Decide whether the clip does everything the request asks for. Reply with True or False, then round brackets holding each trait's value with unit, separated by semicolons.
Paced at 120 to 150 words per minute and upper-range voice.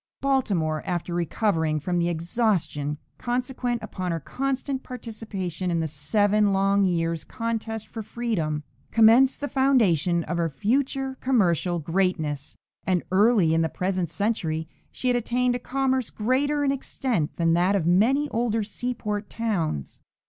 True (140 wpm; 205 Hz)